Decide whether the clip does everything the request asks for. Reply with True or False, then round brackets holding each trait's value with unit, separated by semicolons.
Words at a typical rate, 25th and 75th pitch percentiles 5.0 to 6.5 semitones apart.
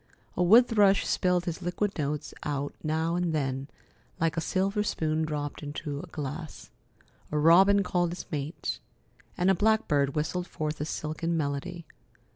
False (155 wpm; 3.3 semitones)